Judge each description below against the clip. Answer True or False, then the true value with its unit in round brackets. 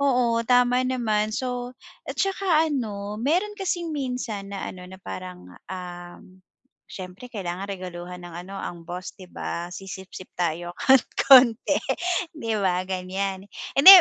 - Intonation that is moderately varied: False (5.7 semitones)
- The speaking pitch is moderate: False (200 Hz)